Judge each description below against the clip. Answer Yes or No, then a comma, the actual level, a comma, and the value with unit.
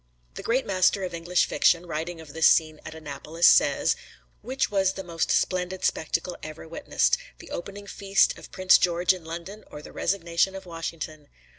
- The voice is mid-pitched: Yes, medium, 175 Hz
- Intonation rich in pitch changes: No, average, 2.9 semitones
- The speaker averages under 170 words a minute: No, average, 175 wpm